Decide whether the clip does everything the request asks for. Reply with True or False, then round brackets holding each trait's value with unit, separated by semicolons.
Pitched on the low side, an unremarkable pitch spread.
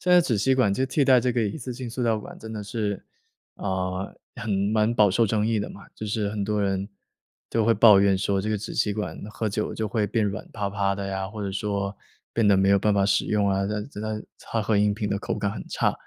False (105 Hz; 2.1 semitones)